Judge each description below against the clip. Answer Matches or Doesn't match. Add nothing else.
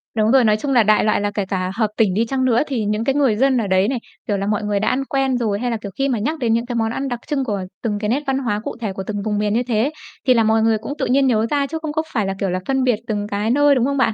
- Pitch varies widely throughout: Doesn't match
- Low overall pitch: Doesn't match